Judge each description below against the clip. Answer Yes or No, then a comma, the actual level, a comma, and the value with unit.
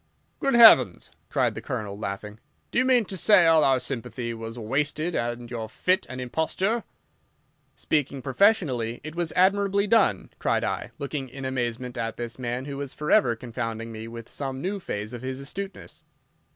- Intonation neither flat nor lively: No, wide, 6.9 semitones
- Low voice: Yes, low, 130 Hz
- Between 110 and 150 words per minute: No, average, 170 wpm